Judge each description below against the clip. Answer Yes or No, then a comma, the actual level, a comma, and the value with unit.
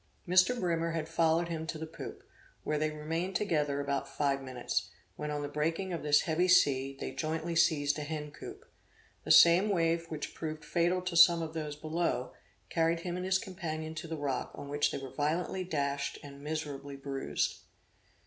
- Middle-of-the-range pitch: Yes, medium, 155 Hz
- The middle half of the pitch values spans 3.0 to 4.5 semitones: No, narrow, 2.6 semitones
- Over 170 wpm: Yes, average, 185 wpm